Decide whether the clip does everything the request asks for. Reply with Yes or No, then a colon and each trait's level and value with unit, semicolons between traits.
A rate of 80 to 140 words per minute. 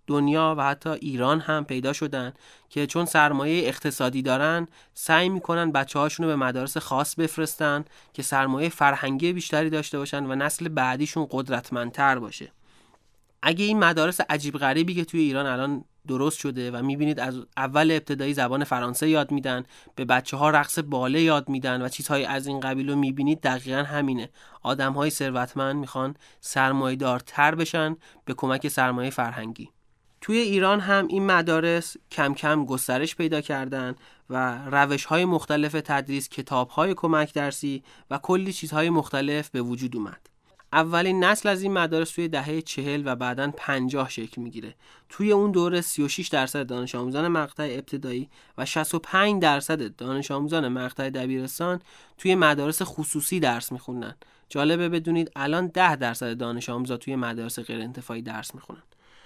No: average, 150 wpm